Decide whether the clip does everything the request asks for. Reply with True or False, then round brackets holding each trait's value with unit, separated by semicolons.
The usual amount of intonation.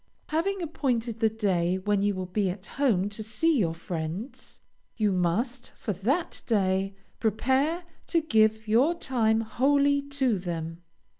False (5.9 semitones)